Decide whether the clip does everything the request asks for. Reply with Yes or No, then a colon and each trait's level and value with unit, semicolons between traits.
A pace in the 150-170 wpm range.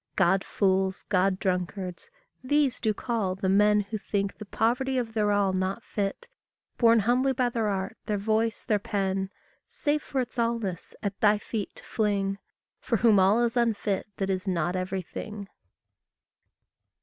Yes: average, 160 wpm